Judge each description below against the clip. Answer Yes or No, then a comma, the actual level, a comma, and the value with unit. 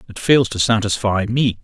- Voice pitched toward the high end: No, low, 110 Hz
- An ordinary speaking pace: Yes, average, 185 wpm